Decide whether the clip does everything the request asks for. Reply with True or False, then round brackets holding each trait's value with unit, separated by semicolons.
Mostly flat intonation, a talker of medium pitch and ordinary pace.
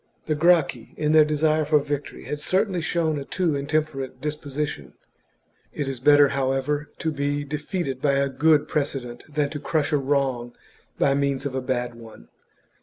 True (2.2 semitones; 145 Hz; 170 wpm)